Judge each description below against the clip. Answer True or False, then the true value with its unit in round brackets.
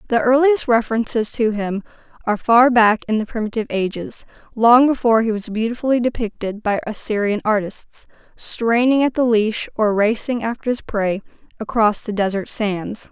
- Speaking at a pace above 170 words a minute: False (155 wpm)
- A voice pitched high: True (225 Hz)